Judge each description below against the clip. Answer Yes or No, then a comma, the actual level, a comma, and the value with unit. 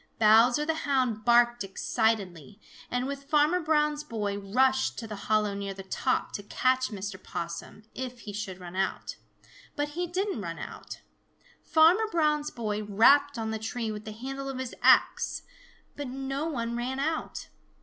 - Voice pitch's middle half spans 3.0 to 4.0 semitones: No, average, 5.3 semitones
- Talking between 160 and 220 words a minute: Yes, average, 165 wpm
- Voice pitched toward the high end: Yes, high, 240 Hz